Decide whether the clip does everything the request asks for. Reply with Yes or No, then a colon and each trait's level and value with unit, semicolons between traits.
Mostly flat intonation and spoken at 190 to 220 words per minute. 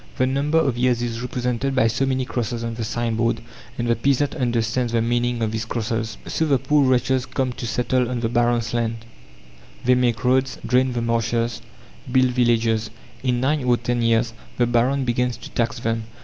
Yes: narrow, 1.7 semitones; average, 195 wpm